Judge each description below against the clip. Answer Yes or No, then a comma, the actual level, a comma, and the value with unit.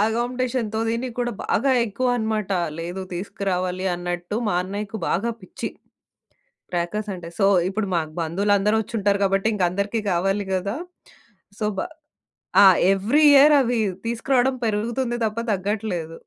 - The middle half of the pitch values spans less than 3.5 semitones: No, average, 3.8 semitones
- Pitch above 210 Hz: No, high, 205 Hz